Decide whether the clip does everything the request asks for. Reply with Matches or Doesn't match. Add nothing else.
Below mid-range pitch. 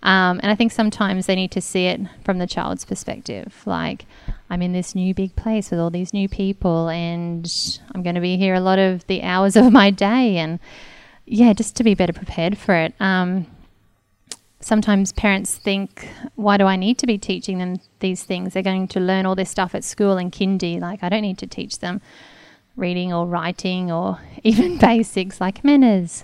Doesn't match